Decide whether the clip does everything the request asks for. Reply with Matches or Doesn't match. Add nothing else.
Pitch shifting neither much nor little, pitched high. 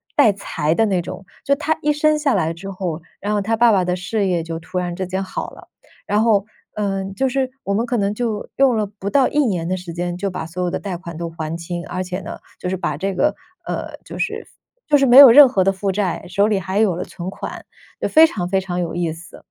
Matches